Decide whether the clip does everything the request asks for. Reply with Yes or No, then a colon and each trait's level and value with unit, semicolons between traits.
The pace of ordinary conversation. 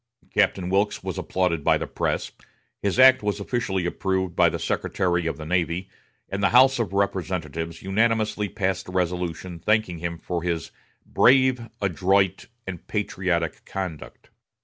Yes: average, 150 wpm